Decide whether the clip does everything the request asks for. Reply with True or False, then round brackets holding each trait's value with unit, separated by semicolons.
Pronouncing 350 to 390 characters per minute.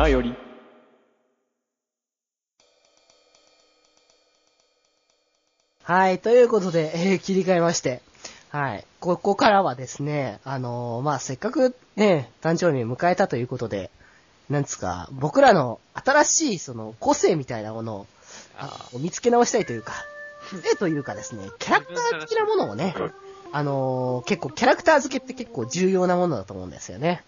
False (300 characters per minute)